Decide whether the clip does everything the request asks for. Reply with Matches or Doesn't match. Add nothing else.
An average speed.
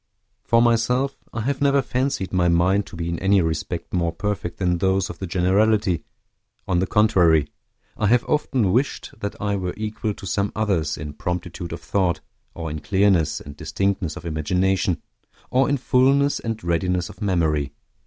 Matches